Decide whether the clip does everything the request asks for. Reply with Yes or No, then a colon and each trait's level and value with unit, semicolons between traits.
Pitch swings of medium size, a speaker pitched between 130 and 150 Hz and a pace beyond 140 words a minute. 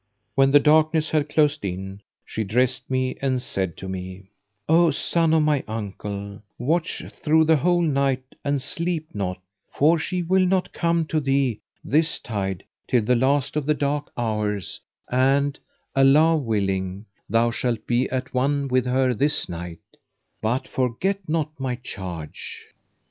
No: wide, 5.9 semitones; low, 135 Hz; average, 155 wpm